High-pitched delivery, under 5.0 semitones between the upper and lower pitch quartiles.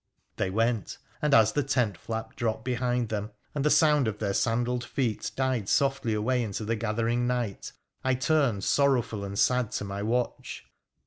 No: low, 120 Hz; average, 3.2 semitones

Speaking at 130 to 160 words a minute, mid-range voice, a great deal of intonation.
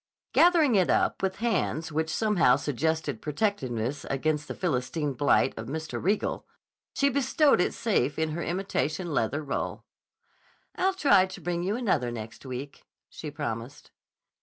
Yes: average, 145 wpm; medium, 160 Hz; wide, 6.2 semitones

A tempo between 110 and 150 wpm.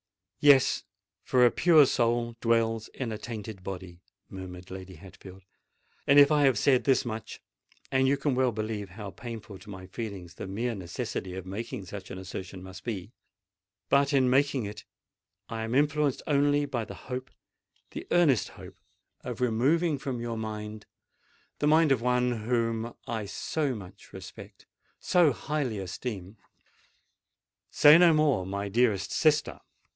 Yes: average, 140 wpm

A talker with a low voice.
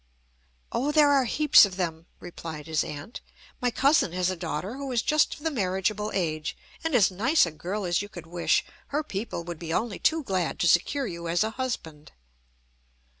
No: high, 190 Hz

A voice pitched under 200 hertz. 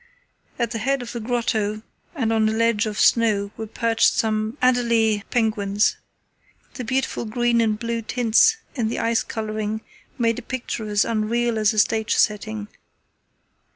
No: high, 225 Hz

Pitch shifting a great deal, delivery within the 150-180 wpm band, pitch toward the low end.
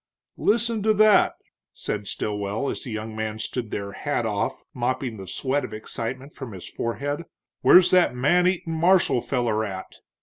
Yes: wide, 7.7 semitones; average, 165 wpm; low, 125 Hz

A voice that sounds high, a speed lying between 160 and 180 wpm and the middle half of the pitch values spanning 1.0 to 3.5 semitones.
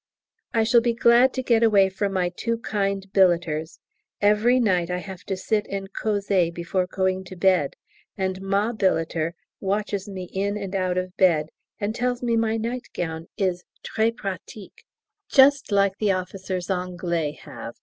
Yes: high, 195 Hz; average, 165 wpm; average, 3.1 semitones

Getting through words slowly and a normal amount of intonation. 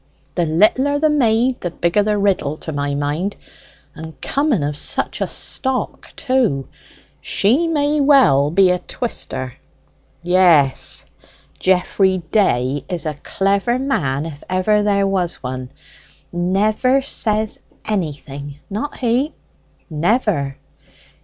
No: slow, 120 wpm; wide, 7.9 semitones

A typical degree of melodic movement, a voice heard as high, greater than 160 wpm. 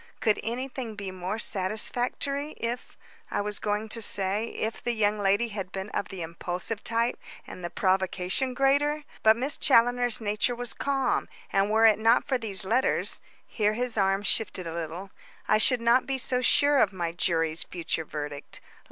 Yes: average, 4.3 semitones; high, 215 Hz; average, 180 wpm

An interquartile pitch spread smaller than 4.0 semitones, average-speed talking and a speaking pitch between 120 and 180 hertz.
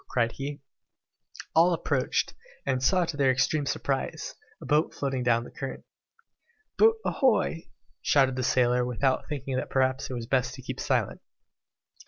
Yes: narrow, 2.6 semitones; average, 160 wpm; low, 135 Hz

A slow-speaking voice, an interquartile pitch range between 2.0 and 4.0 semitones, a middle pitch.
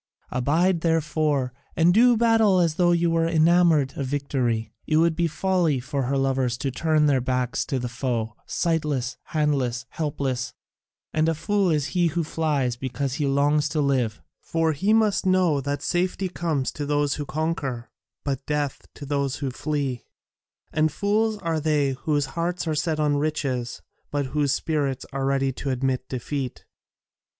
No: average, 165 wpm; average, 3.6 semitones; medium, 145 Hz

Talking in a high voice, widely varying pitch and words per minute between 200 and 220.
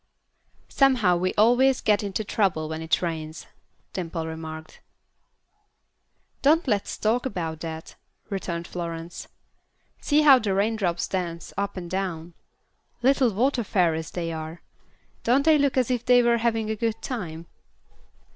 No: high, 195 Hz; wide, 6.2 semitones; slow, 135 wpm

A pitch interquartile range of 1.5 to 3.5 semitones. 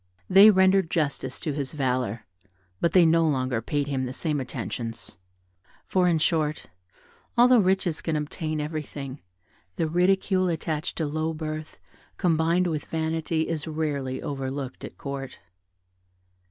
Yes: average, 3.2 semitones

